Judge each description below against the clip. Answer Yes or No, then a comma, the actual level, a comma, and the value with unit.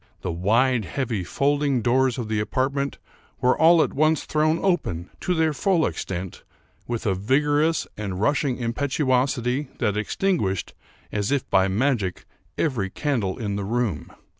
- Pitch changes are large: Yes, wide, 6.0 semitones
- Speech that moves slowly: No, average, 145 wpm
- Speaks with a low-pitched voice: Yes, low, 125 Hz